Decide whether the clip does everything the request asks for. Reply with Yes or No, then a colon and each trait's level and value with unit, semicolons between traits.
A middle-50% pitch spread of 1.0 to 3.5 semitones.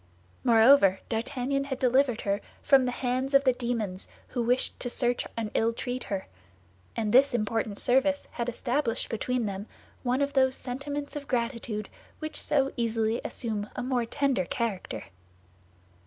Yes: average, 3.0 semitones